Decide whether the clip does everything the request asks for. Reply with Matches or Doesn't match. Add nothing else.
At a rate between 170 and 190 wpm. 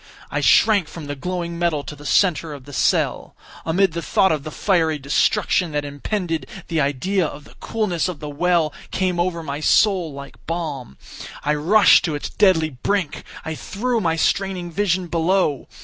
Matches